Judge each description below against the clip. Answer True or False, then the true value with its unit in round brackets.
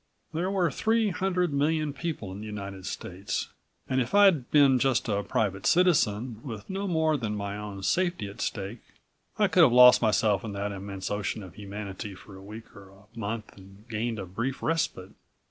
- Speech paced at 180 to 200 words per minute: True (190 wpm)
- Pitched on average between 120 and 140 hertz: False (110 Hz)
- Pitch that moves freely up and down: True (7.2 semitones)